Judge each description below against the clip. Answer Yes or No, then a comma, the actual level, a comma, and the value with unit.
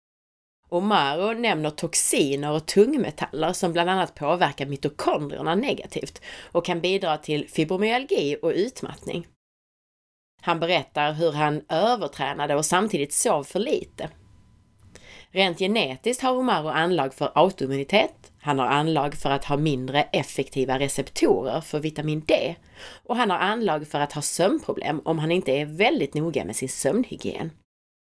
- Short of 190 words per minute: Yes, average, 135 wpm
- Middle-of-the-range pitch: Yes, medium, 155 Hz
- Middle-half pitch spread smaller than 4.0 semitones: No, average, 4.6 semitones